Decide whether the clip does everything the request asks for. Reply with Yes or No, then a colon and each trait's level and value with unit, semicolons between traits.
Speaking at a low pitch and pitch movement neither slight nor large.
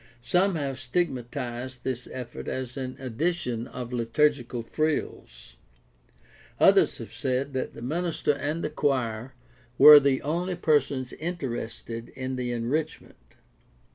Yes: low, 130 Hz; average, 3.7 semitones